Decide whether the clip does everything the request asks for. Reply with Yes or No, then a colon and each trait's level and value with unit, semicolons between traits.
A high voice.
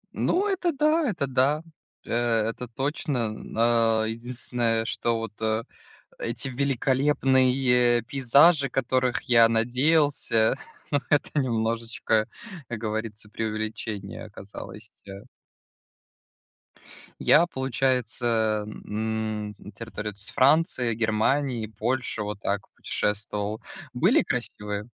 No: low, 115 Hz